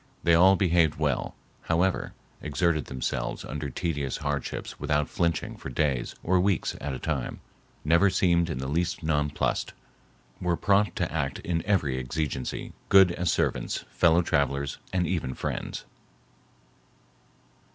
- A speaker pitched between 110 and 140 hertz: No, very low, 80 Hz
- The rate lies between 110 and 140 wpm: Yes, slow, 135 wpm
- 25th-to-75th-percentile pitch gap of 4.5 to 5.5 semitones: No, average, 3.6 semitones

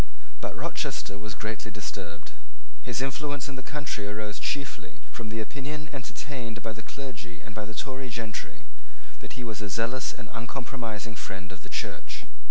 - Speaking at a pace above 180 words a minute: No, average, 170 wpm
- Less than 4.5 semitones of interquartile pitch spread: Yes, average, 3.9 semitones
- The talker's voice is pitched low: Yes, low, 115 Hz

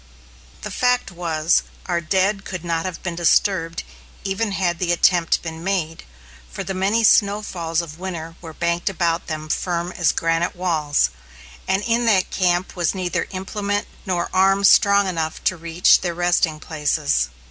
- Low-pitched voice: No, medium, 175 Hz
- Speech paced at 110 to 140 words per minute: No, average, 160 wpm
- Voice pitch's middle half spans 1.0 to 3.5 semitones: Yes, average, 2.7 semitones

